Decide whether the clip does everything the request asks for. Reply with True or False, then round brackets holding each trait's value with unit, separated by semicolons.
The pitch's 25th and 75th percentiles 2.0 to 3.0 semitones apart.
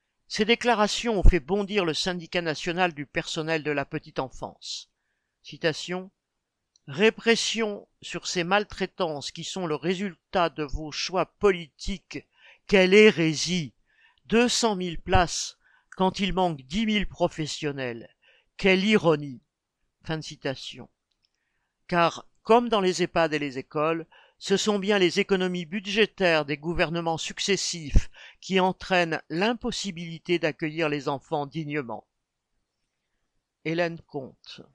False (4.1 semitones)